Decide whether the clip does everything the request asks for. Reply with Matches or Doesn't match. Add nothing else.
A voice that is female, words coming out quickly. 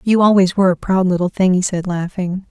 Matches